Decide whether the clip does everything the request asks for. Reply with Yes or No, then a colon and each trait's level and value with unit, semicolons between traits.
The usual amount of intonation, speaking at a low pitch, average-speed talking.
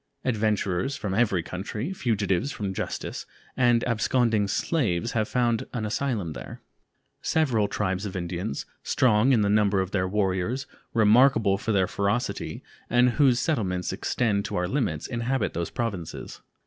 Yes: average, 4.2 semitones; low, 105 Hz; average, 145 wpm